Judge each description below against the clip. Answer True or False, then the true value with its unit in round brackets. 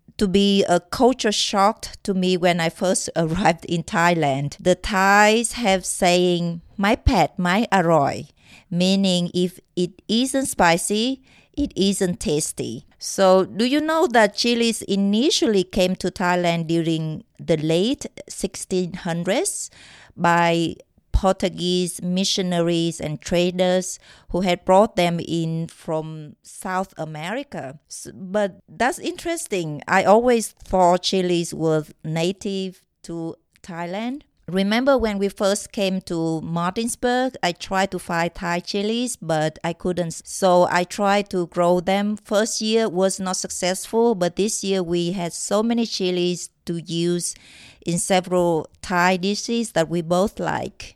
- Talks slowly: True (130 wpm)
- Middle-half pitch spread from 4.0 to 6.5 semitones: False (3.1 semitones)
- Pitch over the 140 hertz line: True (185 Hz)